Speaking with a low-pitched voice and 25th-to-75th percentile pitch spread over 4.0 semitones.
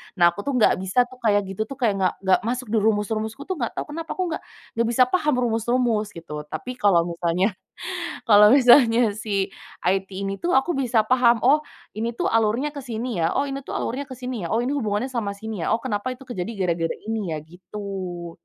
No: high, 225 Hz; average, 4.4 semitones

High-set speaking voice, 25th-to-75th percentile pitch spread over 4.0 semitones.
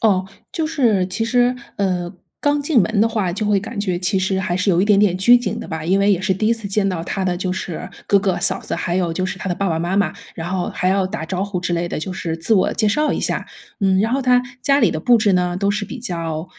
No: high, 195 Hz; average, 3.3 semitones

